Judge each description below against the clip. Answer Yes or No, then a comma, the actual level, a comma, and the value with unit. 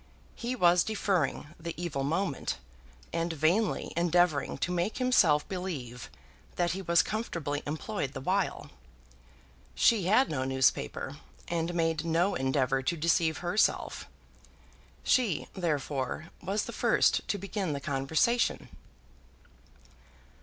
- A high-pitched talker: No, medium, 170 Hz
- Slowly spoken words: Yes, slow, 120 wpm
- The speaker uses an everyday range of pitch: Yes, average, 4.7 semitones